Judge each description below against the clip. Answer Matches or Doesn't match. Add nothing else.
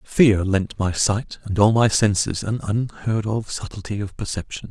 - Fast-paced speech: Doesn't match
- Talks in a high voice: Doesn't match